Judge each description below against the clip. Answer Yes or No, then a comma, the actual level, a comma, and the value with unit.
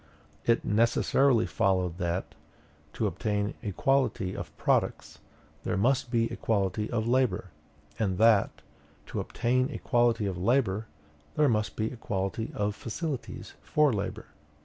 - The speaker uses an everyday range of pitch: Yes, average, 3.8 semitones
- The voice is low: Yes, low, 110 Hz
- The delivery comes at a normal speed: No, slow, 125 wpm